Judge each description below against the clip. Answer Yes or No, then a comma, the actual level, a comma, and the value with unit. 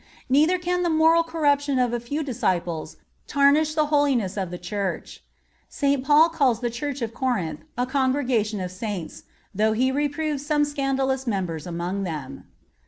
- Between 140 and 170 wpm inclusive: Yes, average, 160 wpm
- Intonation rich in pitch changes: Yes, wide, 6.1 semitones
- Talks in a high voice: Yes, very high, 260 Hz